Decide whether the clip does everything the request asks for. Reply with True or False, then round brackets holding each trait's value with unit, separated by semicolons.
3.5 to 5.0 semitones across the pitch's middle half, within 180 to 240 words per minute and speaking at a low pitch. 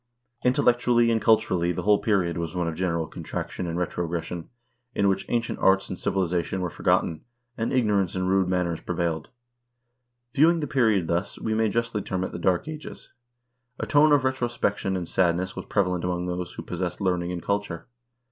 True (4.3 semitones; 185 wpm; 95 Hz)